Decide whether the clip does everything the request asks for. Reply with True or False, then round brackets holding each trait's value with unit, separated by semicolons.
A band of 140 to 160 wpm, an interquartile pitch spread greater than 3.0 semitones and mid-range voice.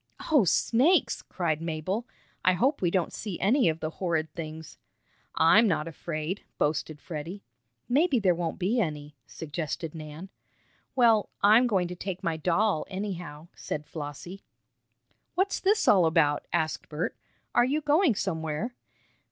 True (145 wpm; 5.4 semitones; 175 Hz)